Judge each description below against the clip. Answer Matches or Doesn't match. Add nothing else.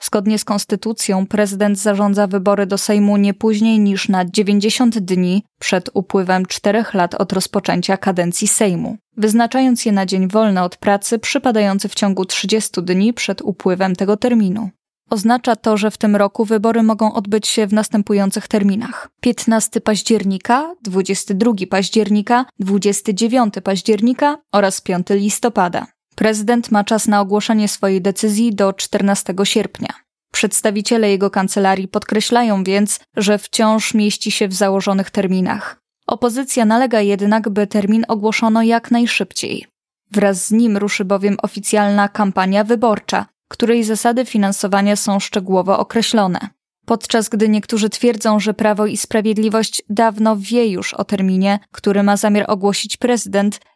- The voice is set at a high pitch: Matches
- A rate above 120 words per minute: Matches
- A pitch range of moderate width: Doesn't match